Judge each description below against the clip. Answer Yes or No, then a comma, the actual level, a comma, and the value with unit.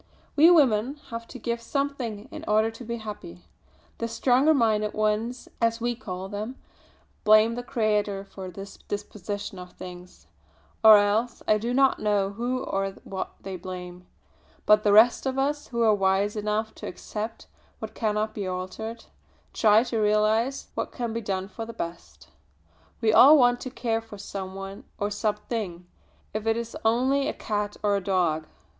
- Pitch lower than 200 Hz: No, high, 215 Hz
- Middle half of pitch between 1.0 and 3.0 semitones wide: Yes, average, 2.7 semitones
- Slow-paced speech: No, average, 170 wpm